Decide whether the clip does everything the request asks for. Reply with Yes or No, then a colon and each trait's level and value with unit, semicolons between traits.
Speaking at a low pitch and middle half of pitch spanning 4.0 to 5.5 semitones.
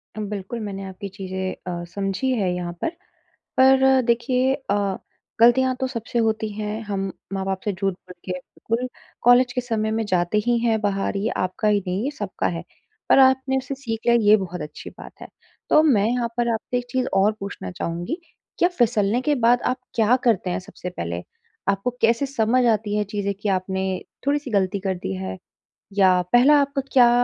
No: high, 220 Hz; average, 4.4 semitones